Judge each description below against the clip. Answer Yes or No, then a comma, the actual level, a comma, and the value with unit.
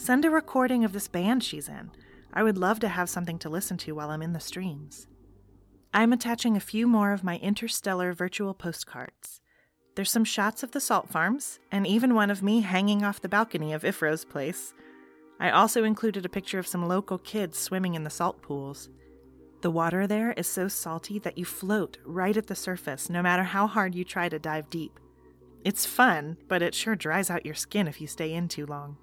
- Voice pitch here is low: No, medium, 185 Hz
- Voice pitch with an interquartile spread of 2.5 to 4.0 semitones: No, average, 4.8 semitones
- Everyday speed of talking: No, fast, 210 wpm